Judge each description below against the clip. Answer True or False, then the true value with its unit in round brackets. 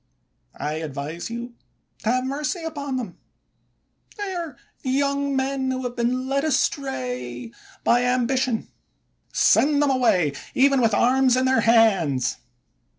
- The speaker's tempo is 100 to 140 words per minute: True (135 wpm)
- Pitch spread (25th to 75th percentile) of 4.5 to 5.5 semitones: False (3.7 semitones)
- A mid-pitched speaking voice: False (255 Hz)